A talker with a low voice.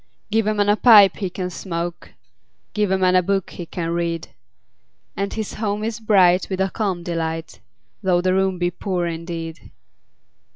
No: medium, 185 Hz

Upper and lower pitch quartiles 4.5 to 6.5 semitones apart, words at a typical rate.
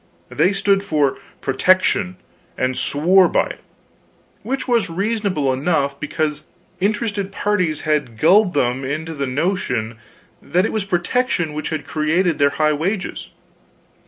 No: average, 5.2 semitones; slow, 130 wpm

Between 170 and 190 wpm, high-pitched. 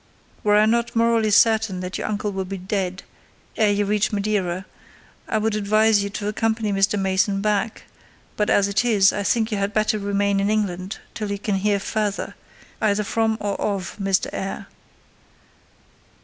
Yes: average, 175 wpm; high, 205 Hz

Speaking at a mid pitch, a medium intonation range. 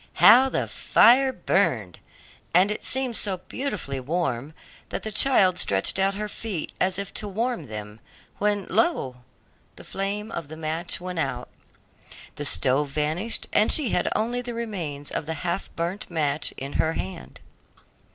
No: medium, 180 Hz; wide, 6.1 semitones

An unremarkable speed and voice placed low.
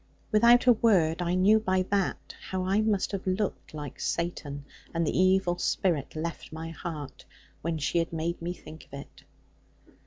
No: average, 175 wpm; medium, 175 Hz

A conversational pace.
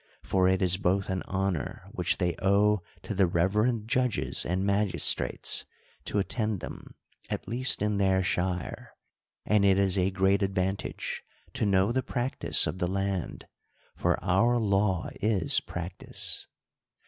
Yes: average, 145 wpm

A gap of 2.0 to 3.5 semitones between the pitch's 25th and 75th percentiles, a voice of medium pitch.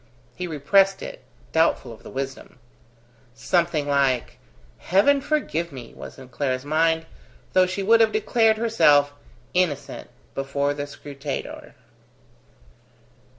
No: wide, 5.6 semitones; medium, 155 Hz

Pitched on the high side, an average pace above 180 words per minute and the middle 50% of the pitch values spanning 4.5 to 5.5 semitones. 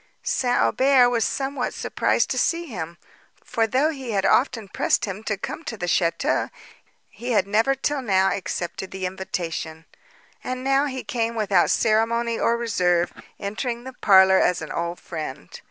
No: high, 220 Hz; average, 165 wpm; average, 5.1 semitones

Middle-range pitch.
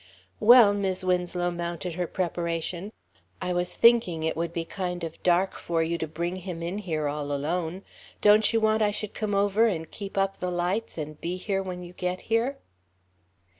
Yes: medium, 180 Hz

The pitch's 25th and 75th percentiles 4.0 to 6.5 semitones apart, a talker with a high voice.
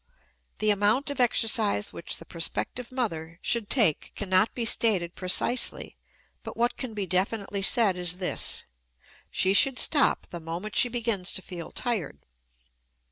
Yes: average, 4.5 semitones; high, 205 Hz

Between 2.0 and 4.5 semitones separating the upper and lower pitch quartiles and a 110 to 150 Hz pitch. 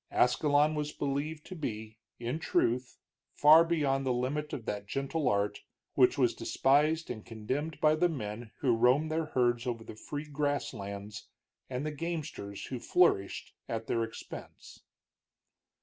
No: average, 5.0 semitones; low, 135 Hz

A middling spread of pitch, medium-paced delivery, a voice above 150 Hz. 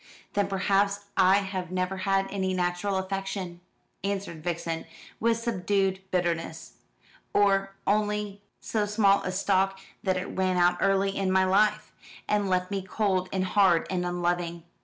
No: narrow, 1.6 semitones; average, 145 wpm; high, 190 Hz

